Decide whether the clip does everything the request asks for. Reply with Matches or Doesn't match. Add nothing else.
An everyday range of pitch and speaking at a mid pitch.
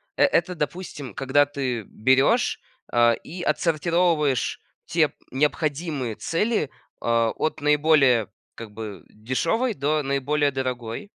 Matches